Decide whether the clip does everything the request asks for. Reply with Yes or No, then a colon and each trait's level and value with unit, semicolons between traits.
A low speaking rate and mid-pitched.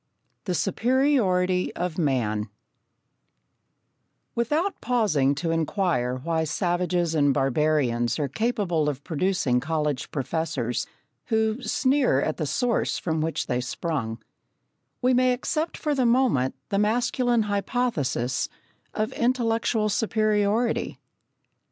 Yes: slow, 110 wpm; medium, 180 Hz